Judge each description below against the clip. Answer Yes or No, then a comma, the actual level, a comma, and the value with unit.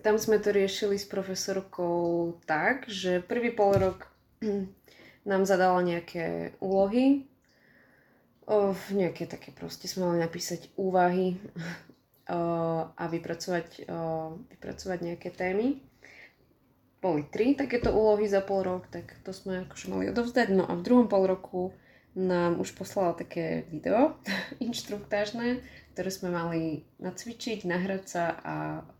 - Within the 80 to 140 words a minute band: Yes, average, 125 wpm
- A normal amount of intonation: Yes, average, 3.2 semitones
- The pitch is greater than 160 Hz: Yes, medium, 185 Hz